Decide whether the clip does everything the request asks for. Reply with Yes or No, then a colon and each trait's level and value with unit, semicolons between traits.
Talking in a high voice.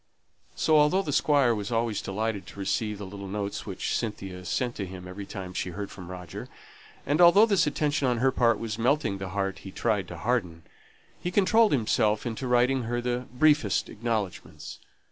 No: low, 110 Hz